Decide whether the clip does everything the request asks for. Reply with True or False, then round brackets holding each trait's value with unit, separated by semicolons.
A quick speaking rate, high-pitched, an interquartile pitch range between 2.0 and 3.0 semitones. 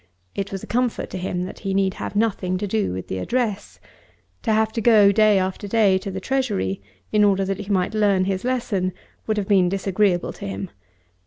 True (215 wpm; 195 Hz; 2.5 semitones)